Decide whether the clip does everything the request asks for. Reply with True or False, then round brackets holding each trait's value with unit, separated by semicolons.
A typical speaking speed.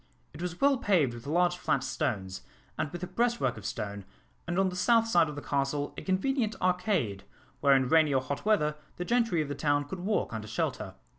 False (215 wpm)